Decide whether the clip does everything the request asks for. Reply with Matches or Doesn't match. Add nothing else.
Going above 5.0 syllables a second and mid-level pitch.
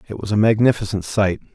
Doesn't match